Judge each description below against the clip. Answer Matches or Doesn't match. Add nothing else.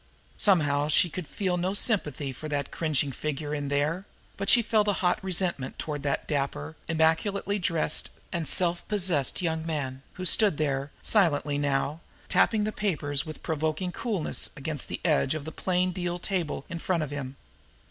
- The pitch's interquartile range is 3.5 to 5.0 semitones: Matches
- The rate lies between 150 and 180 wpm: Matches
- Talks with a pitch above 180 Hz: Doesn't match